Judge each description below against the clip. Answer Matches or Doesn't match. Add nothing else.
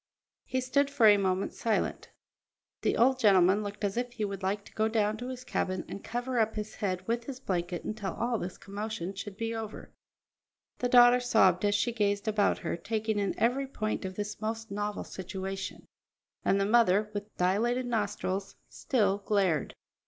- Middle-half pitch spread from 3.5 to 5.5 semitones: Doesn't match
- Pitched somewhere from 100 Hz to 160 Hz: Doesn't match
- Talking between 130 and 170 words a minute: Doesn't match